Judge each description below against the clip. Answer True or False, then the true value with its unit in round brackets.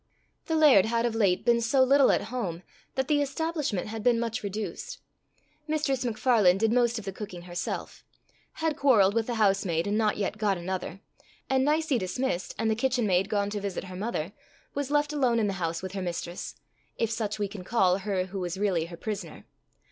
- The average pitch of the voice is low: False (215 Hz)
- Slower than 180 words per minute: False (200 wpm)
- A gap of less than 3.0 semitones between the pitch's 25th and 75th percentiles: False (4.8 semitones)